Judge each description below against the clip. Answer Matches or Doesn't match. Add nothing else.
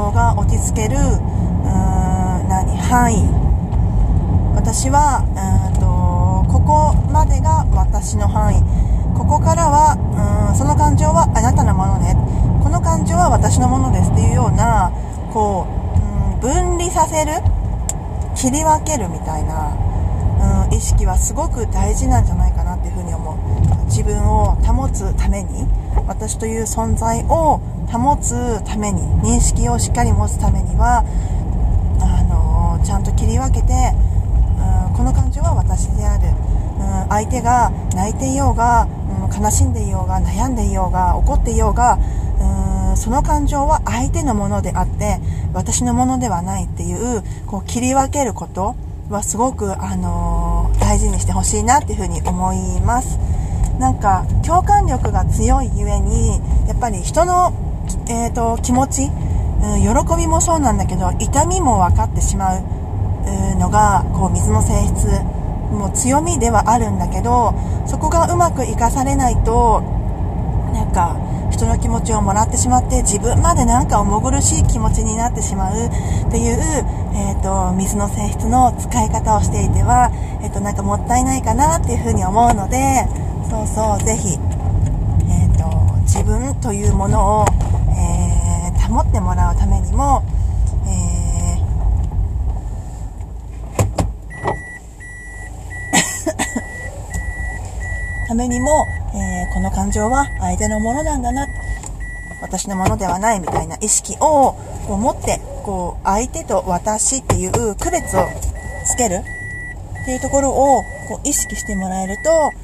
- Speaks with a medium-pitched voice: Doesn't match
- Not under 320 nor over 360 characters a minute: Doesn't match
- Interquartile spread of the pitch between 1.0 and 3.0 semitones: Matches